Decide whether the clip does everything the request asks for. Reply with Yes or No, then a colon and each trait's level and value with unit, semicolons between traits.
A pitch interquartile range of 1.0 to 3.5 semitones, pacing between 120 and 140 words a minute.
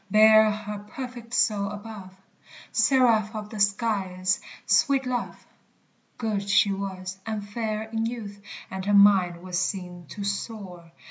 Yes: narrow, 2.4 semitones; slow, 135 wpm